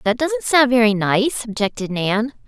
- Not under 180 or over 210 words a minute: No, average, 170 wpm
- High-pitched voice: Yes, high, 215 Hz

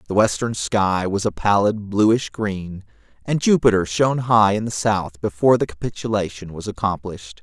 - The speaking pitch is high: No, low, 105 Hz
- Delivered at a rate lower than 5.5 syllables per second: Yes, 5.0 syllables/s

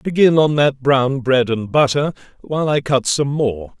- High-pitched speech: No, low, 135 Hz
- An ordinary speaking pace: Yes, average, 190 wpm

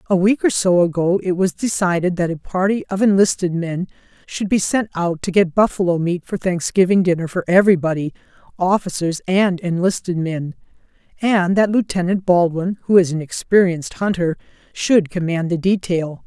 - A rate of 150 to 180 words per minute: Yes, average, 155 wpm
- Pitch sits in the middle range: Yes, medium, 180 Hz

